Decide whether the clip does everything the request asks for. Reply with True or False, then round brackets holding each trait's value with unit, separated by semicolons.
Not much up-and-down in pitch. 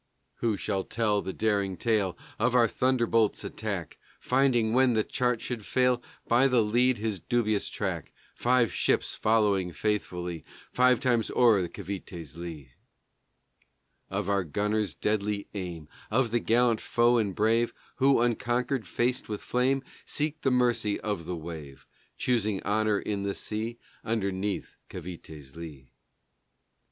False (3.8 semitones)